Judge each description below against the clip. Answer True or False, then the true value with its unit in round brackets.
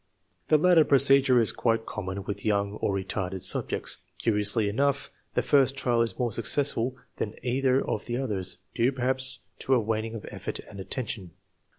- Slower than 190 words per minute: True (170 wpm)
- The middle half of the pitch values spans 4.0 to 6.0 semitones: True (4.3 semitones)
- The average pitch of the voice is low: True (115 Hz)